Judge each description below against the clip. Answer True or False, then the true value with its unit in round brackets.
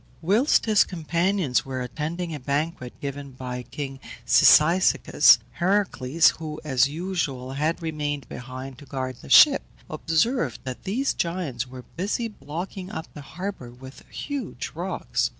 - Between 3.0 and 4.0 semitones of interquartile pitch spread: False (5.4 semitones)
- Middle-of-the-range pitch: True (150 Hz)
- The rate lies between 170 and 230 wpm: False (135 wpm)